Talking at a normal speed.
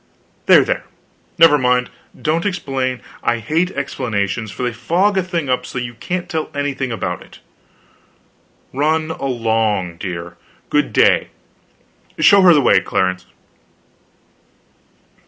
No: slow, 125 wpm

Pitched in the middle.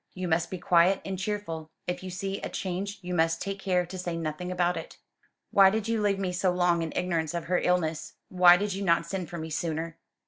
Yes: medium, 180 Hz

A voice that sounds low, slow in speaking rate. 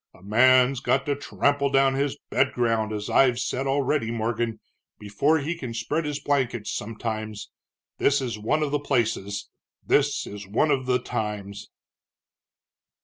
No: low, 125 Hz; average, 150 wpm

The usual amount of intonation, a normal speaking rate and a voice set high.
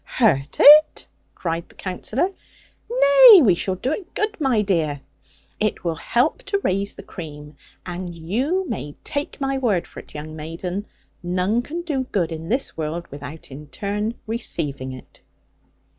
No: wide, 8.9 semitones; average, 160 wpm; high, 195 Hz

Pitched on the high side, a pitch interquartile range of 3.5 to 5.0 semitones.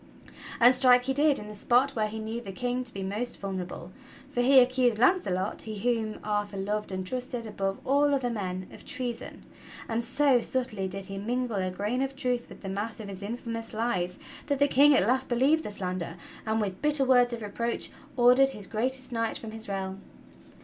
Yes: high, 230 Hz; average, 4.1 semitones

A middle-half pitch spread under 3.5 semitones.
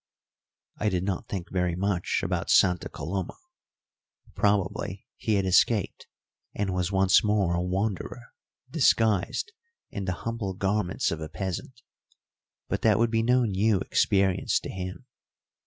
Yes: average, 2.7 semitones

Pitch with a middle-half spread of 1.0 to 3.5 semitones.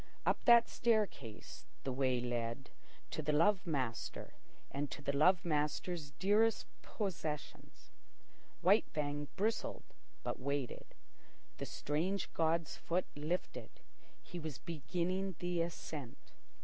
No: average, 4.5 semitones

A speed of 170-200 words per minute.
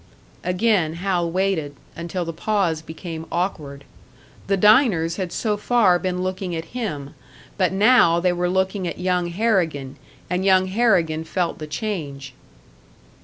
No: average, 140 wpm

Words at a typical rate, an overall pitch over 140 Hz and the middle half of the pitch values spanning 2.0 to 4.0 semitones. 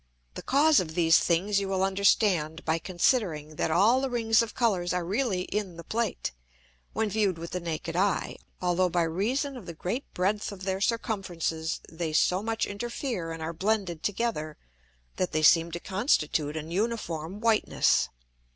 No: average, 170 wpm; medium, 185 Hz; average, 4.8 semitones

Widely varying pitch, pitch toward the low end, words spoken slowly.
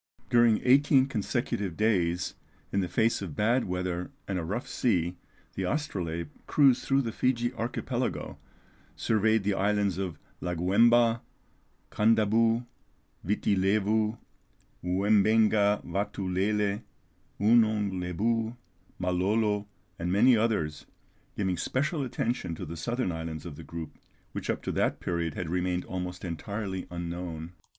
No: average, 4.1 semitones; low, 100 Hz; slow, 125 wpm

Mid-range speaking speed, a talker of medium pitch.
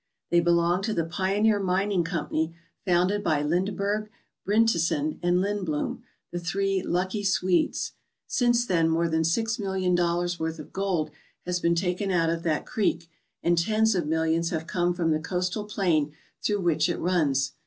Yes: average, 165 wpm; medium, 175 Hz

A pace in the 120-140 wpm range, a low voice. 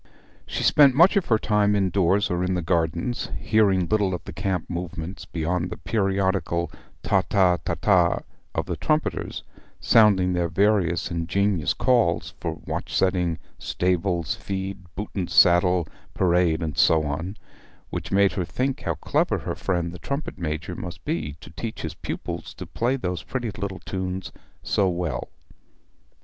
No: average, 160 wpm; very low, 90 Hz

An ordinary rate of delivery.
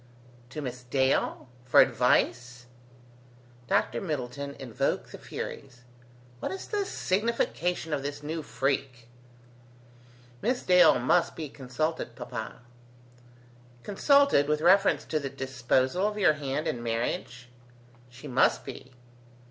No: slow, 115 wpm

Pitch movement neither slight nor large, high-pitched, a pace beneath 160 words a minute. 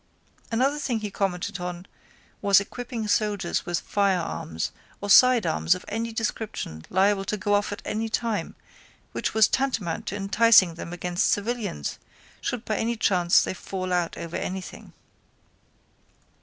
Yes: average, 3.9 semitones; high, 205 Hz; average, 140 wpm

